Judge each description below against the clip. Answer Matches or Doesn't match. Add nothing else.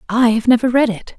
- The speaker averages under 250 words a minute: Doesn't match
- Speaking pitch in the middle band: Doesn't match